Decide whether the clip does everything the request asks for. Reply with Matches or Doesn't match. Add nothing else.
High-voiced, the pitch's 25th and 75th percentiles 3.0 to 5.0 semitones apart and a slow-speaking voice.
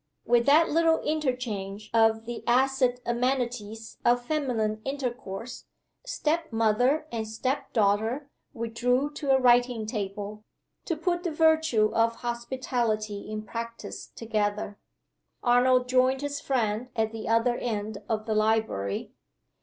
Matches